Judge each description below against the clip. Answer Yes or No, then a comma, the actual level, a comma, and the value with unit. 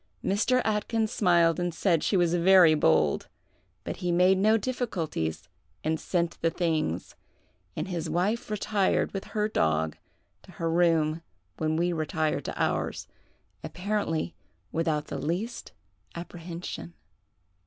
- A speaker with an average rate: No, slow, 125 wpm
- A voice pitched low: No, medium, 170 Hz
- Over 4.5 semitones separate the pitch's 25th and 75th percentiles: No, average, 3.6 semitones